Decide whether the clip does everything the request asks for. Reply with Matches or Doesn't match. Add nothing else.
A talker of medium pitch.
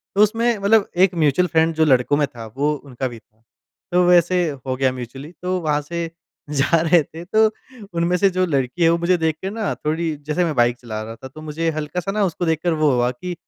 Matches